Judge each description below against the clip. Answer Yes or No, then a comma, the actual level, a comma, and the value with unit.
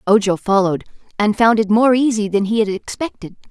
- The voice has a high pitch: Yes, high, 210 Hz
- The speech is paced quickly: No, average, 190 wpm